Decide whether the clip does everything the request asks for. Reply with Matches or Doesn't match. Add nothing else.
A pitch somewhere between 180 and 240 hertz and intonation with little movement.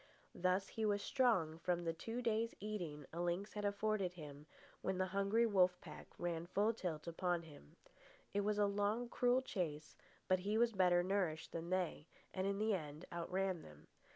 Doesn't match